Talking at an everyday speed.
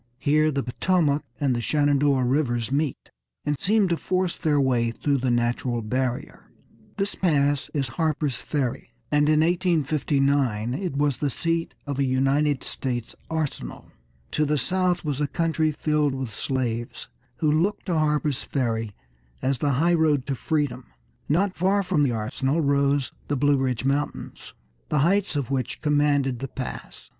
Yes: average, 155 wpm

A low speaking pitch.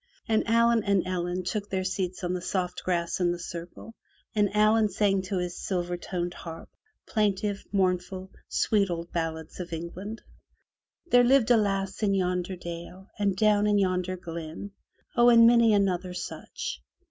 No: high, 190 Hz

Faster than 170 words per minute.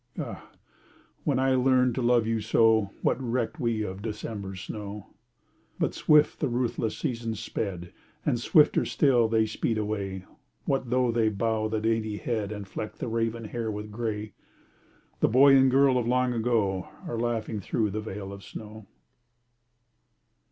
No: average, 160 wpm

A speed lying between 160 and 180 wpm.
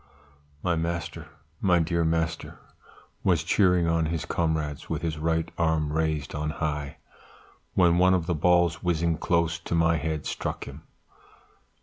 No: average, 145 wpm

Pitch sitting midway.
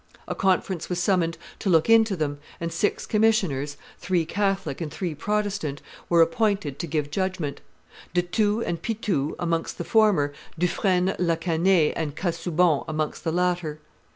Yes: medium, 175 Hz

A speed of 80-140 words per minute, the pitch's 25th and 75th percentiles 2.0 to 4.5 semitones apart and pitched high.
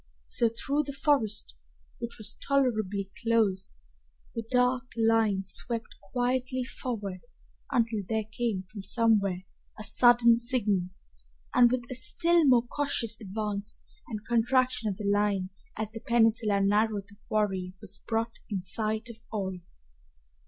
Yes: slow, 135 wpm; average, 3.0 semitones; high, 225 Hz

